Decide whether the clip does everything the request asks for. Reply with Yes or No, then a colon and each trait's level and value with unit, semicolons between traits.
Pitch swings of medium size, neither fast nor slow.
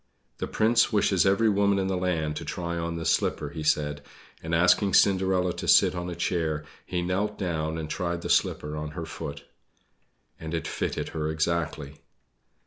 Yes: average, 3.1 semitones; average, 180 wpm